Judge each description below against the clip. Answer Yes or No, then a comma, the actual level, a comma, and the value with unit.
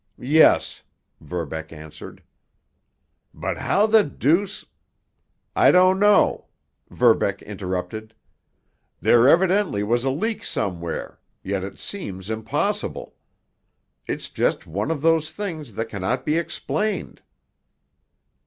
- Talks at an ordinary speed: No, slow, 105 wpm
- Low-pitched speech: Yes, low, 130 Hz